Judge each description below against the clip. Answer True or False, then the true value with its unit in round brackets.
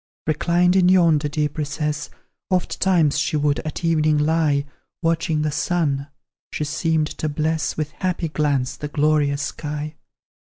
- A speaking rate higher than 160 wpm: False (135 wpm)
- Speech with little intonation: True (1.9 semitones)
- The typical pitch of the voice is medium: True (155 Hz)